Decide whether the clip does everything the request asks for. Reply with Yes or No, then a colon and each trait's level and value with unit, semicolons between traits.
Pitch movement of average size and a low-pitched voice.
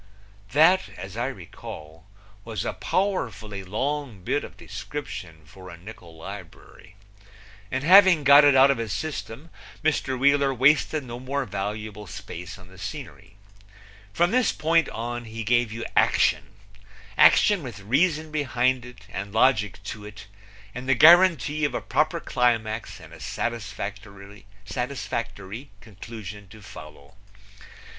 No: wide, 6.0 semitones; low, 115 Hz